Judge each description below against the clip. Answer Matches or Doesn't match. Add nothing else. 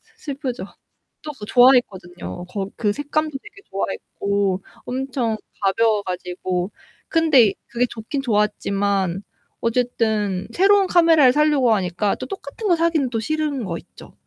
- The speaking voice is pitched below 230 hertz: Doesn't match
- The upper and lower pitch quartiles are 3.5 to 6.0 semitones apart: Doesn't match